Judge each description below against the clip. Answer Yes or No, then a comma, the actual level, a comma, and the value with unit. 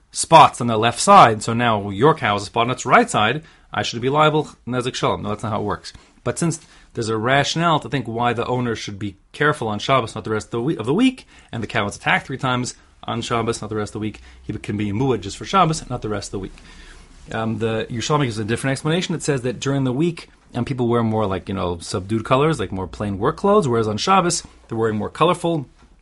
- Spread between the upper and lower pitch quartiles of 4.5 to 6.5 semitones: Yes, average, 4.9 semitones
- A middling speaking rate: No, fast, 260 wpm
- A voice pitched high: No, low, 115 Hz